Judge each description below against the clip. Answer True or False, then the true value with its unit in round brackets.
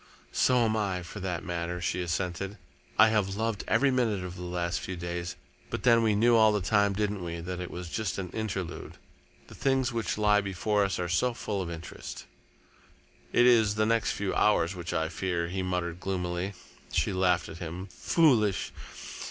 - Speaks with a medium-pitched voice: False (95 Hz)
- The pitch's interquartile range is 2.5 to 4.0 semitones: True (3.6 semitones)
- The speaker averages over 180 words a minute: True (190 wpm)